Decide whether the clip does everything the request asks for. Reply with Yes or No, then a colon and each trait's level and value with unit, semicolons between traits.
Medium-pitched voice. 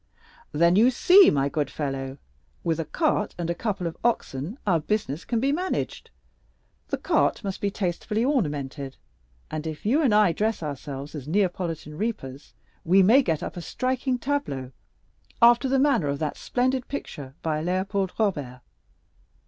Yes: medium, 180 Hz